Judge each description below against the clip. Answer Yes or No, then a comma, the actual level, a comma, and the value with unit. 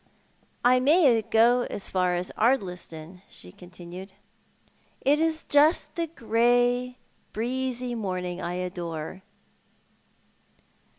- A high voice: Yes, high, 225 Hz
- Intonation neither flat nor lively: No, wide, 5.8 semitones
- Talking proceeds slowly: Yes, slow, 100 wpm